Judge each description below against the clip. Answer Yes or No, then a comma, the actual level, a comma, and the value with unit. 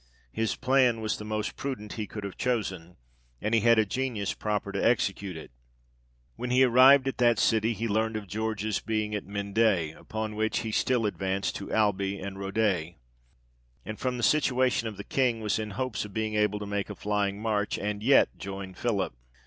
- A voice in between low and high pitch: No, low, 110 Hz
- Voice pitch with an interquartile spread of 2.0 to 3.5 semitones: Yes, narrow, 2.5 semitones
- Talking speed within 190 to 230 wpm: Yes, average, 195 wpm